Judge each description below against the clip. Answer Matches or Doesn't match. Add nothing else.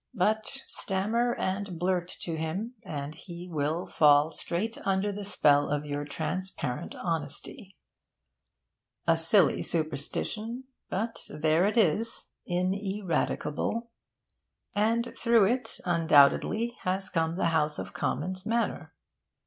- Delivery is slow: Matches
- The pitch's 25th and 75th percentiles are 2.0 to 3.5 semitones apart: Doesn't match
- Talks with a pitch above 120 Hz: Matches